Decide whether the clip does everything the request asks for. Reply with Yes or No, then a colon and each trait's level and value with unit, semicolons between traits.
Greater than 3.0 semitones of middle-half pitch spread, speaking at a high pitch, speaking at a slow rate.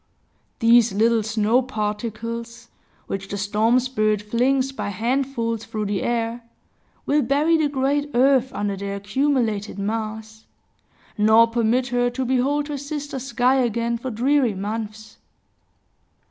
Yes: average, 3.4 semitones; high, 235 Hz; slow, 130 wpm